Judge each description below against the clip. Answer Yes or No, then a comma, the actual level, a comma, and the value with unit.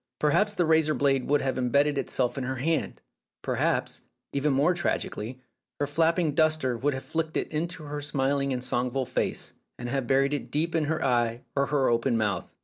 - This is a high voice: No, medium, 140 Hz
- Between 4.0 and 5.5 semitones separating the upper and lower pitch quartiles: No, average, 3.1 semitones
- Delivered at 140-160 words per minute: No, average, 190 wpm